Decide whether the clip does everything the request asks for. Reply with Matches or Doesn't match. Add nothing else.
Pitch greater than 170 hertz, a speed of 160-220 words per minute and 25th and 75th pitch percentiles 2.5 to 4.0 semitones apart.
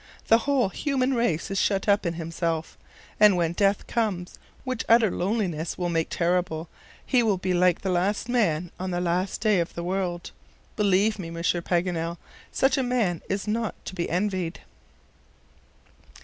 Matches